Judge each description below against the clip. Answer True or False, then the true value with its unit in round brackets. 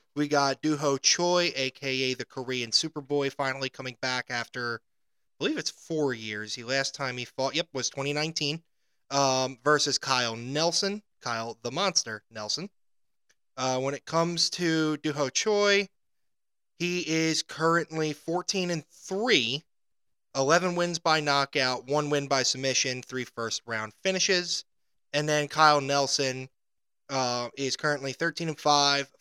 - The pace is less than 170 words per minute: True (140 wpm)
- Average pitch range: True (3.7 semitones)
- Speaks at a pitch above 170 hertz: False (140 Hz)